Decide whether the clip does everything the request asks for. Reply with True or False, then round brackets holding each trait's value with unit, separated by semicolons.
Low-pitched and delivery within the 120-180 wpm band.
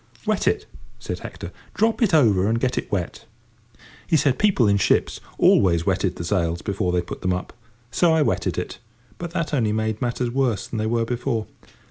False (115 Hz; 195 wpm)